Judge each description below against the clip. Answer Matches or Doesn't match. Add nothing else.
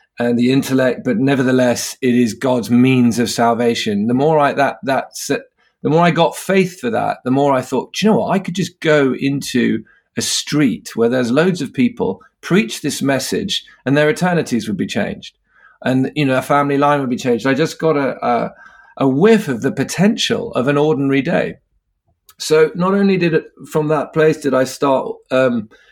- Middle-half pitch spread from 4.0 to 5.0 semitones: Matches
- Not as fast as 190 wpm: Doesn't match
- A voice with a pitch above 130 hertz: Matches